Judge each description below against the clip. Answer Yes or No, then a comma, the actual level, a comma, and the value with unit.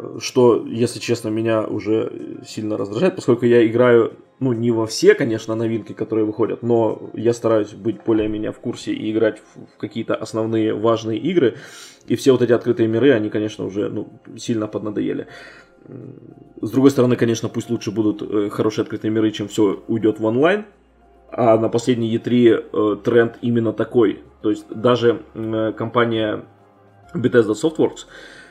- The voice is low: Yes, low, 115 Hz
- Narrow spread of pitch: Yes, narrow, 1.5 semitones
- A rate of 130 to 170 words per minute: Yes, average, 150 wpm